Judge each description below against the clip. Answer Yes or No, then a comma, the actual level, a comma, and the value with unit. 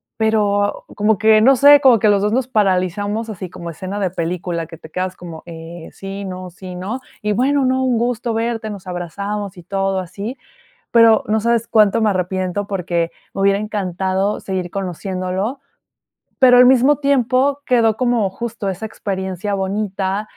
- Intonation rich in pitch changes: No, average, 3.6 semitones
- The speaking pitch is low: No, high, 205 Hz